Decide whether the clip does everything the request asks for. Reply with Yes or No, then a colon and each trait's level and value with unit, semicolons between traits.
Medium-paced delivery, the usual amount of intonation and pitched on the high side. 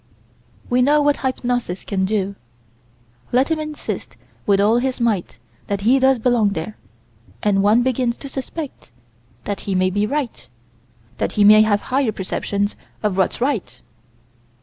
Yes: average, 150 wpm; average, 4.5 semitones; high, 220 Hz